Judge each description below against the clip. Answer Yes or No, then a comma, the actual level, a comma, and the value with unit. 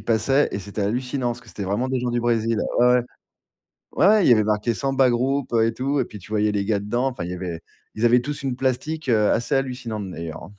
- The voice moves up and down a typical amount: Yes, average, 3.8 semitones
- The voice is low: Yes, low, 120 Hz